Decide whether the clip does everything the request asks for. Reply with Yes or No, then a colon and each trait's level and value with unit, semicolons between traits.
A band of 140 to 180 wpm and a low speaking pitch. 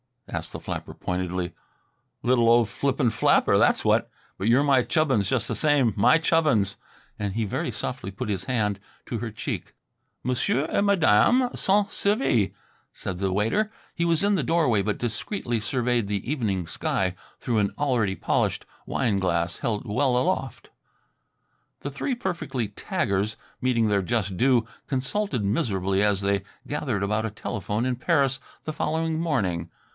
Yes: average, 155 wpm; low, 120 Hz